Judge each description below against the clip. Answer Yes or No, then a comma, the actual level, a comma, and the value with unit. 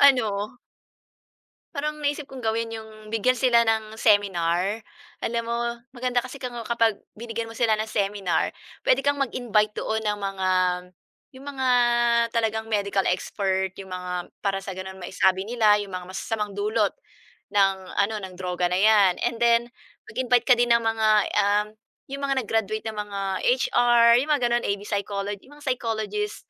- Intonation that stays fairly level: No, average, 3.2 semitones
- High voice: Yes, high, 220 Hz